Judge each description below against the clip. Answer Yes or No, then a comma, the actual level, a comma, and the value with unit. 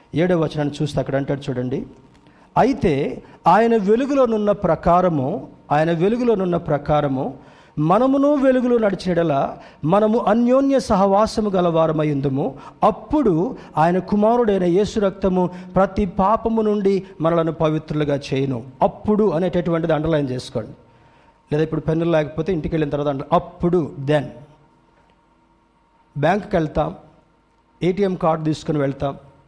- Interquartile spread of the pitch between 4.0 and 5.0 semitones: Yes, average, 4.7 semitones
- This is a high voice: No, medium, 165 Hz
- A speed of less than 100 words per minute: No, average, 105 wpm